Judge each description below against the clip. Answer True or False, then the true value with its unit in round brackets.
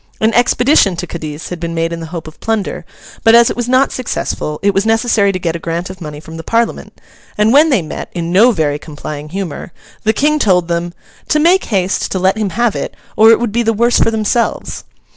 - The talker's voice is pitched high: True (195 Hz)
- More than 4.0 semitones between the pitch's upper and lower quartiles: True (5.6 semitones)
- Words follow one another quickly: True (235 wpm)